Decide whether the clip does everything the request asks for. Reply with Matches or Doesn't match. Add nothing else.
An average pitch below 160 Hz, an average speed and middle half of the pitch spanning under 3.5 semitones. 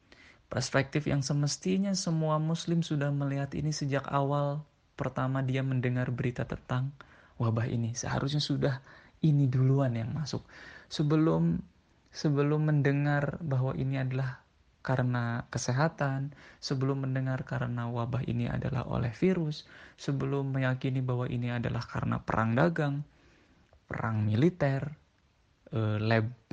Matches